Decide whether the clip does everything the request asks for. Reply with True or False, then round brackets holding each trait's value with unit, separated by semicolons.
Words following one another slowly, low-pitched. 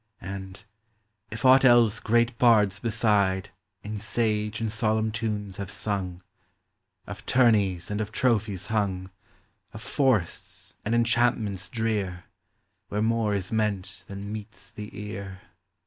True (130 wpm; 105 Hz)